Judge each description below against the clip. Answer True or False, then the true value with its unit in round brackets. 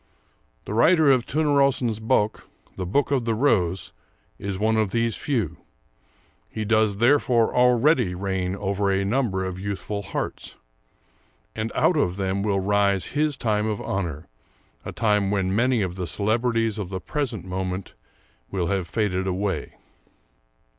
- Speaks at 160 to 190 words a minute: False (145 wpm)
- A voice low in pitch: True (105 Hz)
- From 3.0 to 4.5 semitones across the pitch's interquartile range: True (3.6 semitones)